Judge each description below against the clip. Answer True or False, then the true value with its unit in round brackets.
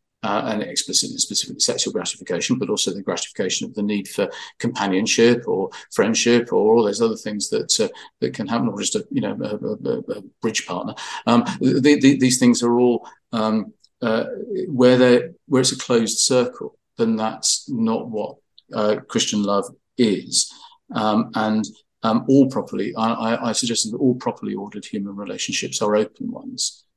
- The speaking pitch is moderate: False (120 Hz)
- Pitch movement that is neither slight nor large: True (3.6 semitones)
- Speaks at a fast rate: False (175 wpm)